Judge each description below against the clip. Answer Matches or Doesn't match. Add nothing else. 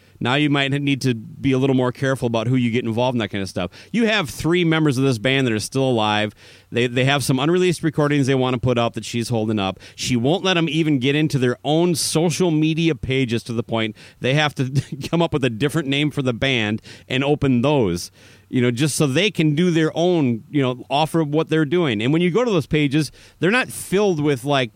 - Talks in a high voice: Doesn't match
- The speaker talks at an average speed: Doesn't match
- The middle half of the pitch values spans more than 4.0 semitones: Matches